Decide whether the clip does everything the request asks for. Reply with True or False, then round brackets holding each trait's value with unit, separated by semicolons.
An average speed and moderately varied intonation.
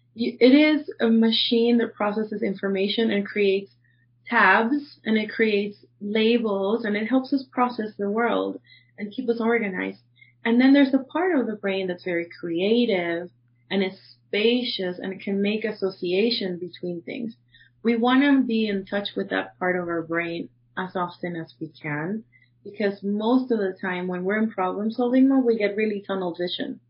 True (180 wpm; 4.6 semitones)